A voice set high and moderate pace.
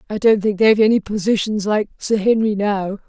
Yes: high, 210 Hz; average, 195 wpm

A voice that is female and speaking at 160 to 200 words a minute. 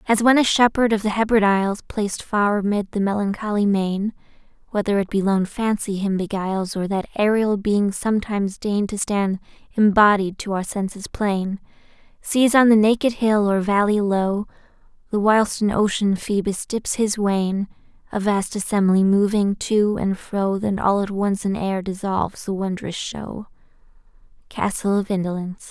Yes: female; average, 165 wpm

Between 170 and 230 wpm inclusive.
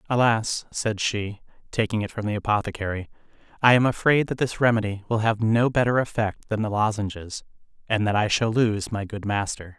Yes: average, 185 wpm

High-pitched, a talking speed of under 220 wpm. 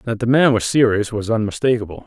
No: low, 115 Hz; fast, 205 wpm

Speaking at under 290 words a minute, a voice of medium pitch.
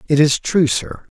Yes: average, 200 wpm; medium, 155 Hz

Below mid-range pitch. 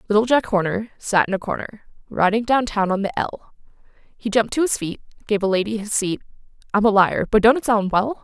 No: high, 215 Hz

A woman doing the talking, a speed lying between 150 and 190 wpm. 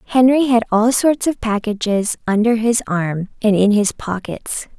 Yes: female; average, 165 wpm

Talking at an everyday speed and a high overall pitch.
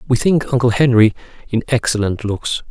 No: average, 155 wpm; low, 120 Hz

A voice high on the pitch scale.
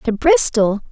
Yes: very high, 250 Hz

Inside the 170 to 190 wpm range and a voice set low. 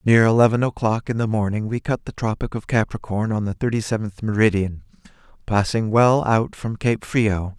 Yes: average, 180 wpm; low, 110 Hz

